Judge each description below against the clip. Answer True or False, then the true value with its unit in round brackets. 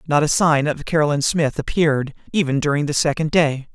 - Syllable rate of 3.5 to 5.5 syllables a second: False (5.9 syllables/s)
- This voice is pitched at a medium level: True (150 Hz)